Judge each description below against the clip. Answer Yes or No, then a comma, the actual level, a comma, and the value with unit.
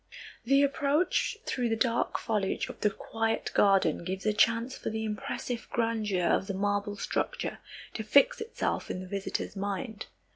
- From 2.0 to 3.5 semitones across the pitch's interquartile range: Yes, average, 3.0 semitones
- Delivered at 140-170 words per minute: Yes, average, 160 wpm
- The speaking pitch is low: No, high, 220 Hz